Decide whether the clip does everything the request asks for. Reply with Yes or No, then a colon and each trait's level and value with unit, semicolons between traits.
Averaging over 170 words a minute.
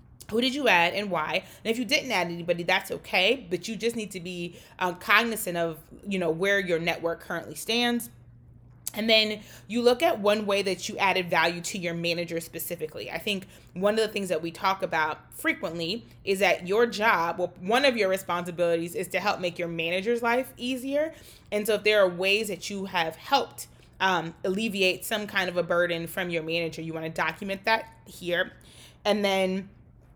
Yes: average, 200 wpm